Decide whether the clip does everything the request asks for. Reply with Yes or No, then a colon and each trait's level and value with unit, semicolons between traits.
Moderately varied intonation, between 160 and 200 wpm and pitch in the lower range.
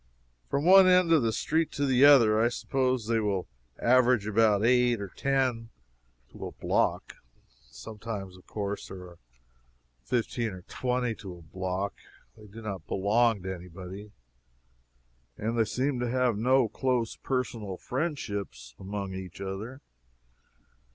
No: average, 4.6 semitones; average, 145 wpm; low, 110 Hz